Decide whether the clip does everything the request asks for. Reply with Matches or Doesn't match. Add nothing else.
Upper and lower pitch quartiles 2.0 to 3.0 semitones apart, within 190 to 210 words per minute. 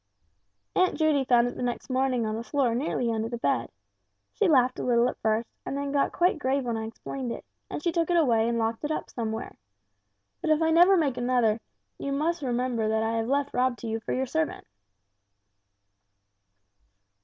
Doesn't match